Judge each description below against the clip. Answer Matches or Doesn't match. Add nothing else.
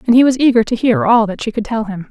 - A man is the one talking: Doesn't match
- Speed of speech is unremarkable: Doesn't match